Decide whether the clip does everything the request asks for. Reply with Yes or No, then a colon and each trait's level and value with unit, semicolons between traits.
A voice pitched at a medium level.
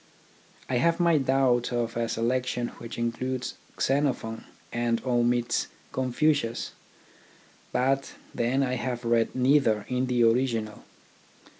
No: low, 125 Hz